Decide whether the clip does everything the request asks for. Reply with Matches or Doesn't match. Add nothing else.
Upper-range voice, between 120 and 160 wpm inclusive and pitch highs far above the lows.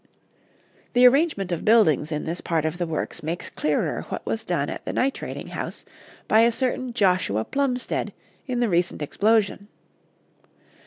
Matches